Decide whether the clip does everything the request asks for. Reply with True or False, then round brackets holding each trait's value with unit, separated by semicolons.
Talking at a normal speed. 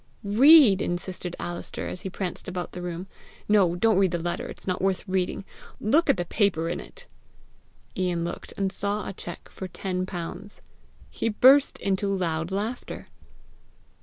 True (165 wpm)